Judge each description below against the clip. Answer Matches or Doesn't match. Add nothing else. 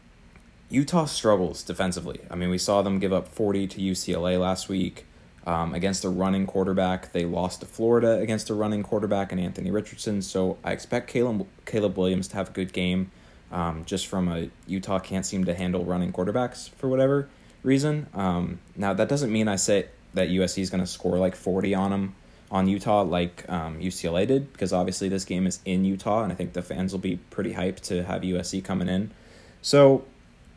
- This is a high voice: Doesn't match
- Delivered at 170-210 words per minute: Matches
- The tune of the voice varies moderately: Doesn't match